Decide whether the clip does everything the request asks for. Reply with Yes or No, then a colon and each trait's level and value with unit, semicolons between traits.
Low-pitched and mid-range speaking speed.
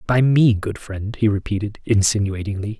Yes: low, 105 Hz; average, 150 wpm